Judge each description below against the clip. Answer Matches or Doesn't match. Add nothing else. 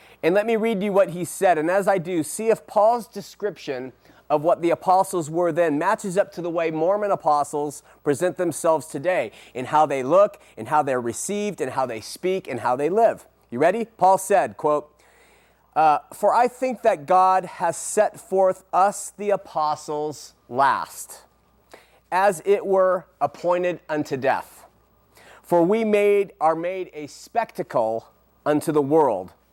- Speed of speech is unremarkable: Matches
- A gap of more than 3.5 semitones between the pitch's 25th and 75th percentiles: Matches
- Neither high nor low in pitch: Matches